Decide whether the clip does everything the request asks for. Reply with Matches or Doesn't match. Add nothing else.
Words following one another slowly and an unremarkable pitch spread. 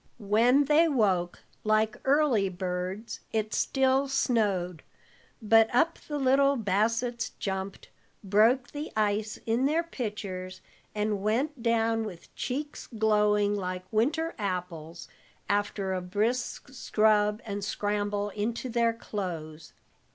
Matches